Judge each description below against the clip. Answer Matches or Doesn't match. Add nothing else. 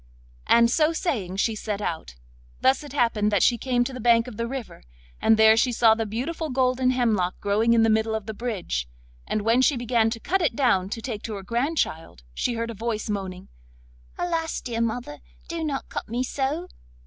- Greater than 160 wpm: Matches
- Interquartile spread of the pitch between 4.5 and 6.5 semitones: Doesn't match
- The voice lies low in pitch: Doesn't match